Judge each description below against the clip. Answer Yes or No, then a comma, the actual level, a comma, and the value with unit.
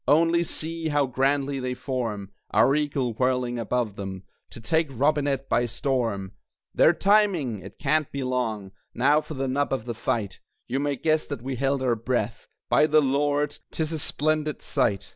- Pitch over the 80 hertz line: Yes, low, 135 Hz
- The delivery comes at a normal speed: Yes, average, 175 wpm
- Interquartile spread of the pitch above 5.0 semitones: No, average, 3.8 semitones